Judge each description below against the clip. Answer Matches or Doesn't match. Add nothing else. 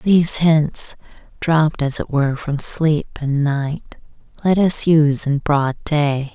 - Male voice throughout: Doesn't match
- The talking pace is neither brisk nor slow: Matches